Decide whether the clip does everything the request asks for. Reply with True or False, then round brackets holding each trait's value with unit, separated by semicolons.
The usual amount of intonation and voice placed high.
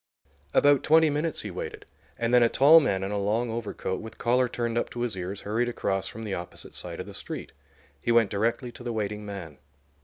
False (3.3 semitones; 115 Hz)